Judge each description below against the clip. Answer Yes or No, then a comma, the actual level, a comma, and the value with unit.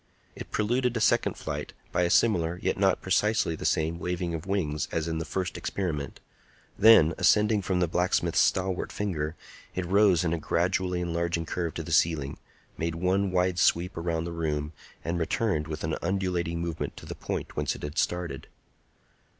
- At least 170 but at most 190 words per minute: Yes, average, 180 wpm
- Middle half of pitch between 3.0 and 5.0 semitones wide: No, narrow, 2.5 semitones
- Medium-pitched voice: No, very low, 85 Hz